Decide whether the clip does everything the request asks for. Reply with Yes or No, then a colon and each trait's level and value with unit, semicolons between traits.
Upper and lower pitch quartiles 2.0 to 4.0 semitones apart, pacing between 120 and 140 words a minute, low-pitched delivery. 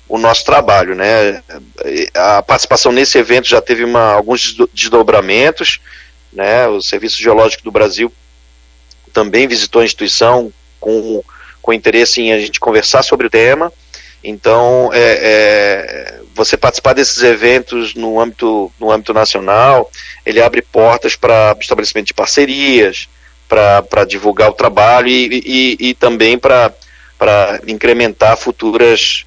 Yes: average, 2.9 semitones; average, 130 wpm; low, 115 Hz